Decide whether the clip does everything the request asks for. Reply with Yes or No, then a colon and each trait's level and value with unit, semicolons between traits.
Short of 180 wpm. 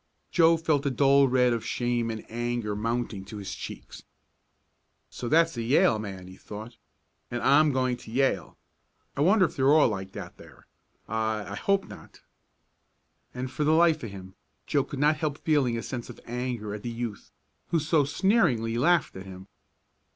No: average, 185 wpm